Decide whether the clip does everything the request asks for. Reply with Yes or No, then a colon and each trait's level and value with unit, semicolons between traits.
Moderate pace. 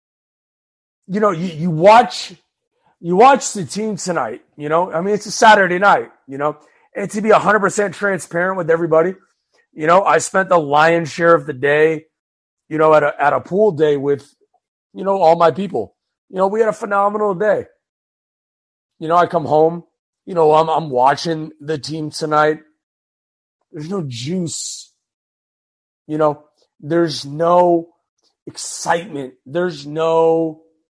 Yes: average, 160 wpm